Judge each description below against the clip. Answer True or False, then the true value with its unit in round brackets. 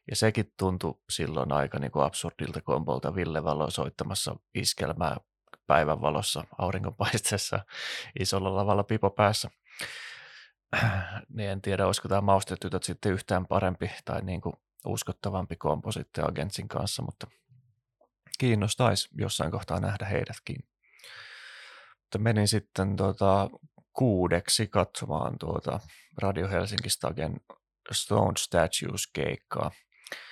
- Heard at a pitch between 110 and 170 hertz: False (95 Hz)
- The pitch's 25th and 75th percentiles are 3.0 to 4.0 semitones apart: True (3.6 semitones)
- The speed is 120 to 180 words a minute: False (105 wpm)